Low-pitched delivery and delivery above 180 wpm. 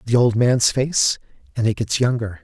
Yes: low, 115 Hz; average, 200 wpm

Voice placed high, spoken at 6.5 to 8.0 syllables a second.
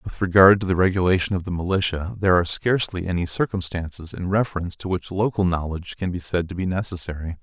No: very low, 90 Hz; 6.6 syllables/s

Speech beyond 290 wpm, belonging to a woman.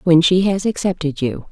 No: average, 200 wpm; female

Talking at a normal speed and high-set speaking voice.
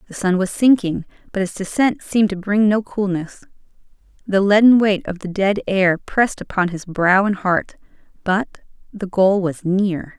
Yes: average, 175 wpm; high, 195 Hz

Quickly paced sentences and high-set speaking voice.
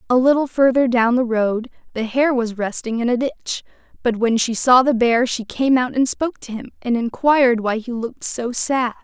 Yes: fast, 220 wpm; high, 245 Hz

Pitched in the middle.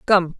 Yes: medium, 180 Hz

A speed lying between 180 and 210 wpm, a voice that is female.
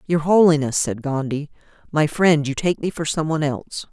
Yes: average, 200 wpm; female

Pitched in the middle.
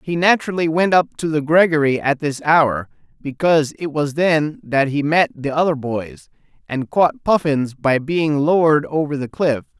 Yes: medium, 155 Hz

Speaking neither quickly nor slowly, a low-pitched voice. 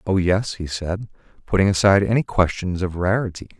Yes: average, 165 wpm; very low, 95 Hz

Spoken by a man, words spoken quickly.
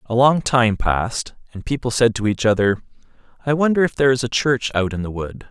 Yes: male; fast, 220 wpm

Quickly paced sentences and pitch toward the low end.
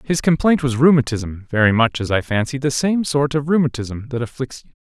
Yes: fast, 210 wpm; low, 130 Hz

